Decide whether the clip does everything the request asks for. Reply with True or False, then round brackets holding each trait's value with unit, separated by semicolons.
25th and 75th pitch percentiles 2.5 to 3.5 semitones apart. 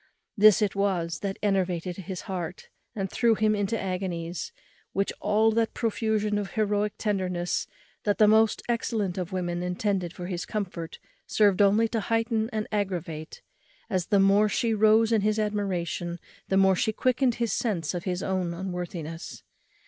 True (3.1 semitones)